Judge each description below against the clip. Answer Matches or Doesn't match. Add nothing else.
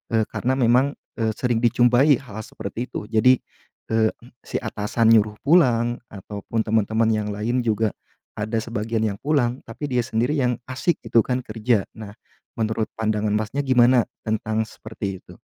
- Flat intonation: Matches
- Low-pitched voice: Matches